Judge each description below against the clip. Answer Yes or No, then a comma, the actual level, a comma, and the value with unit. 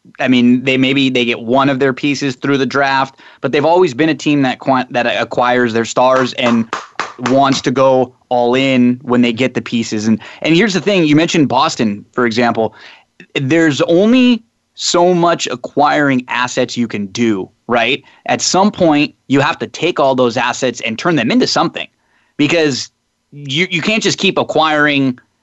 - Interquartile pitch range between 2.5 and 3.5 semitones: No, average, 3.9 semitones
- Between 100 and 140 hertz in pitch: Yes, low, 135 Hz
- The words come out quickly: No, average, 185 wpm